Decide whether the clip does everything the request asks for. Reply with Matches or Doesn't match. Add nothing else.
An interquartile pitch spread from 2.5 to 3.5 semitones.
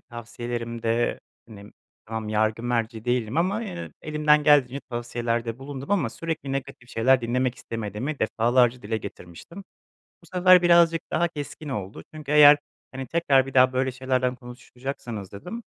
Doesn't match